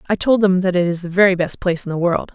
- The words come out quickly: Yes, fast, 335 wpm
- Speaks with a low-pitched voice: No, medium, 185 Hz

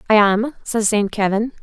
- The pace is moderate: Yes, average, 185 wpm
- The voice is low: No, high, 215 Hz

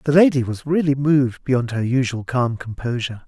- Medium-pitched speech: No, low, 130 Hz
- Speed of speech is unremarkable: Yes, average, 185 wpm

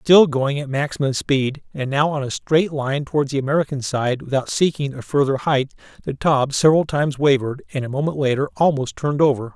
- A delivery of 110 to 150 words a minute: No, average, 200 wpm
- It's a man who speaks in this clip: Yes, male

